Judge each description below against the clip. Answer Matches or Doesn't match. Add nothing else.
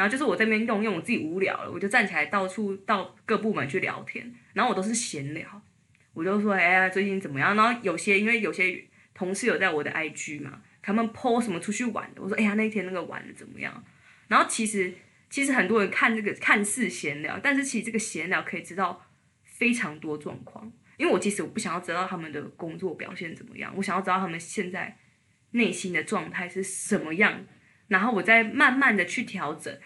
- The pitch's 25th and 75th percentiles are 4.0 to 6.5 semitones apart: Doesn't match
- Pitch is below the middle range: Doesn't match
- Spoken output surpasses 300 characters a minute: Matches